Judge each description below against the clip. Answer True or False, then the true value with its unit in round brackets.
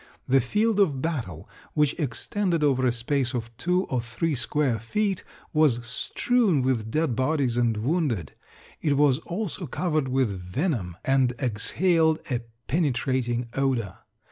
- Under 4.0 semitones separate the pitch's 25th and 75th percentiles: False (5.2 semitones)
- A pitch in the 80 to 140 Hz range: True (135 Hz)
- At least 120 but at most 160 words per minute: True (140 wpm)